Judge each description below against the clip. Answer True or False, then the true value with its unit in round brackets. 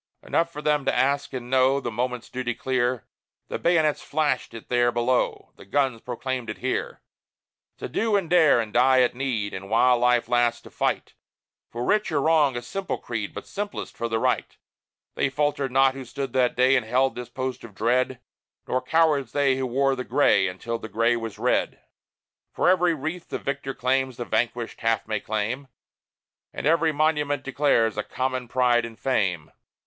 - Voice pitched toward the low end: True (130 Hz)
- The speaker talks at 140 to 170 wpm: False (185 wpm)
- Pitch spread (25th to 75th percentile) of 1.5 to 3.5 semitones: True (3.0 semitones)